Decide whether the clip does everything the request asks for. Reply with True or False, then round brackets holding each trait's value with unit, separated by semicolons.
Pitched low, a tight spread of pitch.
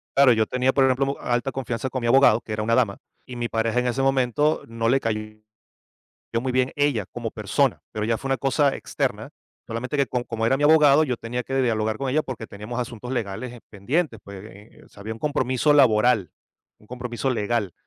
False (125 Hz; 3.1 semitones)